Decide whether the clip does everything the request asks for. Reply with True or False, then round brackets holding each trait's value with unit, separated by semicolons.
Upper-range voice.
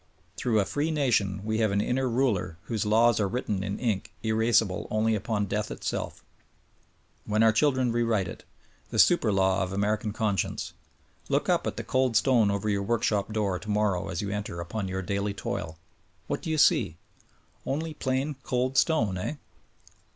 False (110 Hz)